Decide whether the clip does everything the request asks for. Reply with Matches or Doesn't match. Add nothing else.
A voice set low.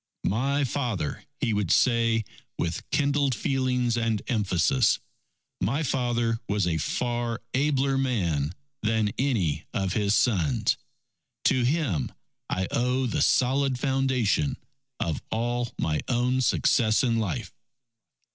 Matches